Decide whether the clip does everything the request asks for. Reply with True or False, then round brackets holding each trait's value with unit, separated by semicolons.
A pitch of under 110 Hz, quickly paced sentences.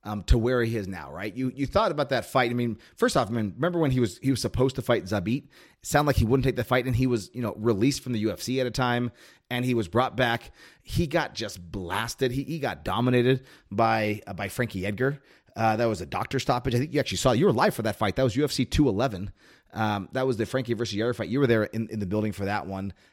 False (120 Hz; 270 wpm)